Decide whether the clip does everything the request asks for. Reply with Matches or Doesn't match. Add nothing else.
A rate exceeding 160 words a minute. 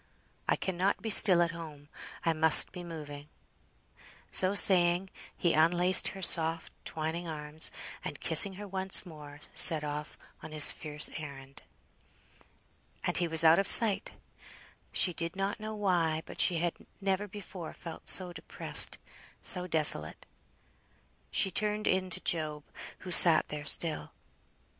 Doesn't match